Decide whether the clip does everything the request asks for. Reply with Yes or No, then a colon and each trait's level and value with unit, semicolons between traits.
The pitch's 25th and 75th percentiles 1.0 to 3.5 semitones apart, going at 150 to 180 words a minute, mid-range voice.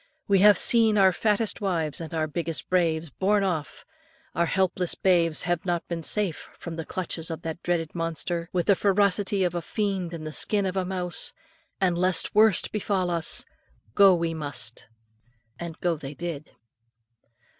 Yes: average, 2.8 semitones; average, 170 wpm; medium, 175 Hz